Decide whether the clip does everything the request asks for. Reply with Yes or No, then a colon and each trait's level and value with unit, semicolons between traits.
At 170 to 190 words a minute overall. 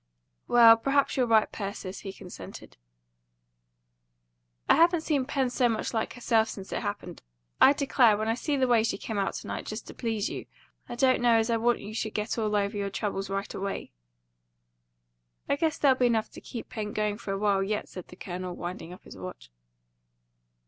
No: average, 200 wpm